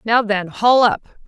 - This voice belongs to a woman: Yes, female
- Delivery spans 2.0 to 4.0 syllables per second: Yes, 3.6 syllables/s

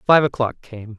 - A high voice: No, low, 125 Hz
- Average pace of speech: Yes, average, 185 wpm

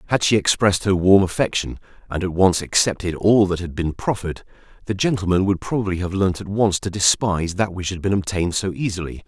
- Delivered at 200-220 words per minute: Yes, fast, 205 wpm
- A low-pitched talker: Yes, very low, 95 Hz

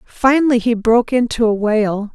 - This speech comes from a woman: Yes, female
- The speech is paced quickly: No, average, 170 wpm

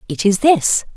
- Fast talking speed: No, average, 190 wpm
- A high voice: Yes, high, 220 Hz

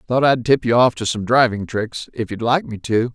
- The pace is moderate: No, fast, 250 wpm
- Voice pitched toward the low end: Yes, low, 120 Hz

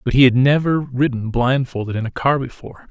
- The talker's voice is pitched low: Yes, low, 130 Hz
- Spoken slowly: No, fast, 205 wpm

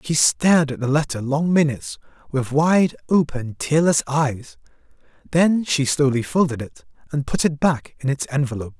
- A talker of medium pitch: Yes, medium, 145 Hz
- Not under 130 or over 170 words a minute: Yes, average, 165 wpm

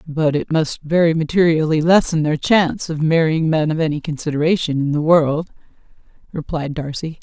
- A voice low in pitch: No, medium, 155 Hz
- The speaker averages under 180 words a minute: Yes, average, 160 wpm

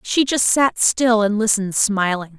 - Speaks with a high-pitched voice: Yes, high, 215 Hz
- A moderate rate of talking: Yes, average, 175 wpm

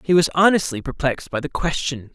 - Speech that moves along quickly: No, average, 195 wpm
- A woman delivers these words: No, male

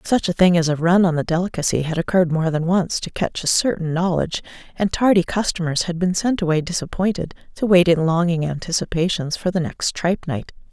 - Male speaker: No, female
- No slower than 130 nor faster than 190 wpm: No, average, 200 wpm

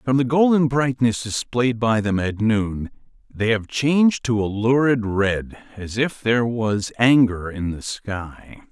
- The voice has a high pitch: No, low, 115 Hz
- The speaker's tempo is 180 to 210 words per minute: No, average, 160 wpm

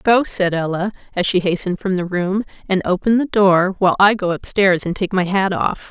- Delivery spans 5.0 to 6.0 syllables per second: Yes, 5.3 syllables/s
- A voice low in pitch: No, high, 190 Hz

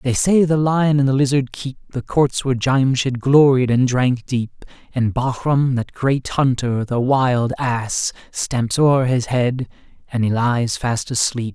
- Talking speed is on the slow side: No, average, 165 wpm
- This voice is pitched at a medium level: No, low, 130 Hz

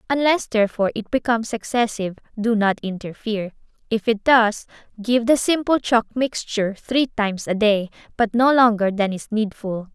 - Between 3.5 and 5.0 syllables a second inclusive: No, 5.2 syllables/s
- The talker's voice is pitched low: No, high, 225 Hz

